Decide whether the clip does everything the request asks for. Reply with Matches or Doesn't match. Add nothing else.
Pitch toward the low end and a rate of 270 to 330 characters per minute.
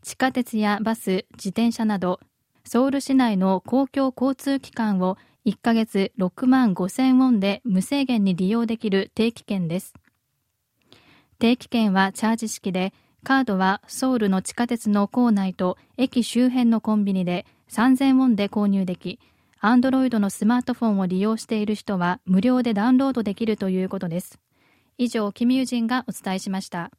Doesn't match